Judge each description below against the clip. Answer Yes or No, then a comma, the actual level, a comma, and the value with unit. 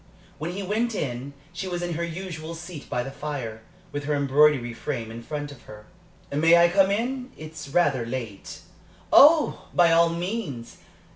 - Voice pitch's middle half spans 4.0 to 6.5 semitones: Yes, average, 4.6 semitones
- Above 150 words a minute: Yes, average, 180 wpm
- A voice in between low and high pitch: Yes, medium, 155 Hz